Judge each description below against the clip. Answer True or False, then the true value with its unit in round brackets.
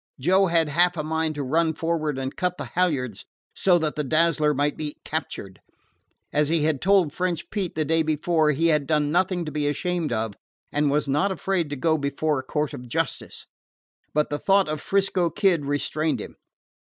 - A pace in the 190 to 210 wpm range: True (195 wpm)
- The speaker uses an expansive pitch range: False (2.8 semitones)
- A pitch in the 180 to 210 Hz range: False (155 Hz)